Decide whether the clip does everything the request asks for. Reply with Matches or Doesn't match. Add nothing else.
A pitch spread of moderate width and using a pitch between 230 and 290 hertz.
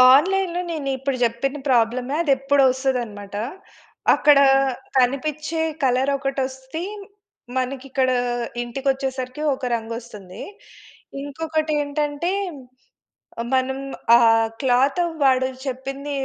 Doesn't match